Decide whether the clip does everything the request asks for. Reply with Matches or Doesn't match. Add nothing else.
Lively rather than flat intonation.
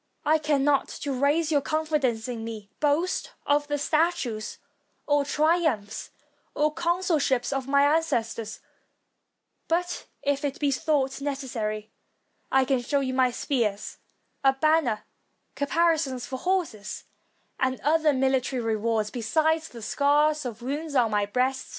Doesn't match